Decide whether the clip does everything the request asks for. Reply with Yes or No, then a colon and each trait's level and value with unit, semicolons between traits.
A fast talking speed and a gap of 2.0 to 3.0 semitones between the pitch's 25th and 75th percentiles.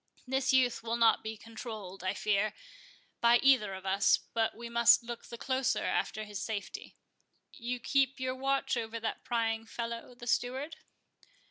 No: average, 160 wpm; narrow, 2.5 semitones